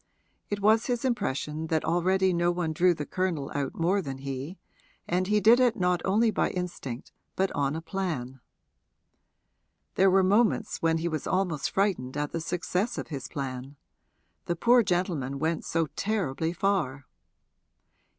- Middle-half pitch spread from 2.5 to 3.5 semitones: No, average, 4.7 semitones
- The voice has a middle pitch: Yes, medium, 175 Hz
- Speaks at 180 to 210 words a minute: No, average, 160 wpm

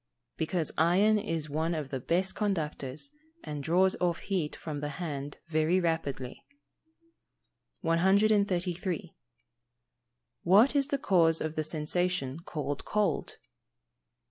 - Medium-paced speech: No, slow, 115 wpm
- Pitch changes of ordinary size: Yes, average, 3.7 semitones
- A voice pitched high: No, medium, 170 Hz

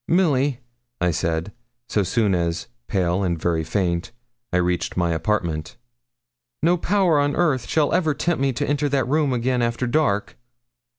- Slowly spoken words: No, average, 160 wpm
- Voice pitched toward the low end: Yes, low, 120 Hz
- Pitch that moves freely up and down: Yes, wide, 8.6 semitones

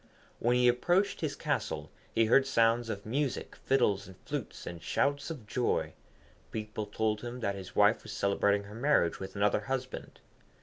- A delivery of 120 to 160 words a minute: No, average, 170 wpm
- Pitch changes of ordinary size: Yes, average, 4.4 semitones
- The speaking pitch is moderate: No, low, 115 Hz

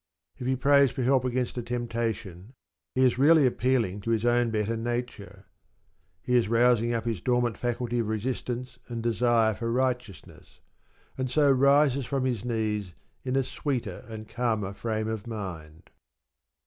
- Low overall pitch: Yes, low, 120 Hz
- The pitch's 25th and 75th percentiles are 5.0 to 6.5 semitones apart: No, narrow, 2.4 semitones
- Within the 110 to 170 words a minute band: Yes, average, 160 wpm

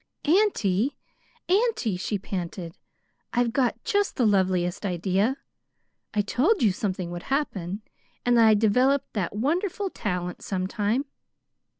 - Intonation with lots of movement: Yes, wide, 6.4 semitones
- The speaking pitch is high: Yes, high, 215 Hz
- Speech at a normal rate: No, slow, 120 wpm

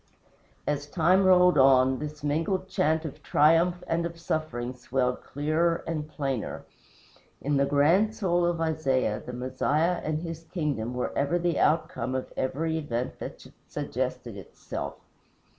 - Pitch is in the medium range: Yes, medium, 155 Hz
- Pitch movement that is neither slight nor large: Yes, average, 4.0 semitones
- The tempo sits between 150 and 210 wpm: No, average, 140 wpm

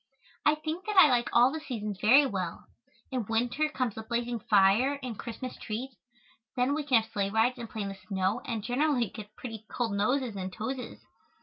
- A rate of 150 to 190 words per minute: No, average, 200 wpm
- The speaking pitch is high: Yes, high, 235 Hz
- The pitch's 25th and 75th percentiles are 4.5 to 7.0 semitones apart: No, average, 3.8 semitones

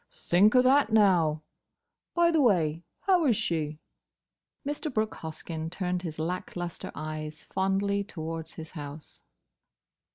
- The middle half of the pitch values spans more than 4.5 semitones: Yes, average, 5.2 semitones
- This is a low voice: No, medium, 175 Hz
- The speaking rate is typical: No, slow, 125 wpm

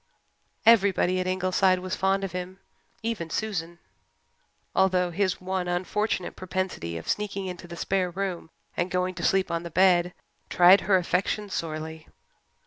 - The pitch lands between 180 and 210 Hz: Yes, medium, 185 Hz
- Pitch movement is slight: Yes, narrow, 1.6 semitones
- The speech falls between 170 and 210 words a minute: No, average, 145 wpm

